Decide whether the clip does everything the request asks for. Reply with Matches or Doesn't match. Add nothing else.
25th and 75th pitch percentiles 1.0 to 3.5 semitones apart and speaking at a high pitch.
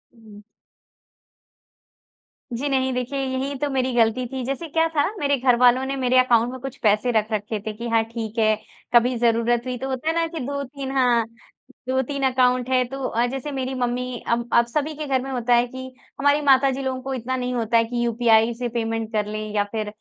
Matches